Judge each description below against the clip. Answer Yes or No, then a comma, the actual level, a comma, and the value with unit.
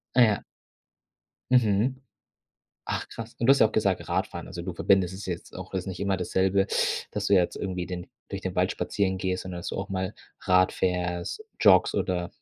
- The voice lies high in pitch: No, very low, 95 Hz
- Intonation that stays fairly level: Yes, narrow, 2.0 semitones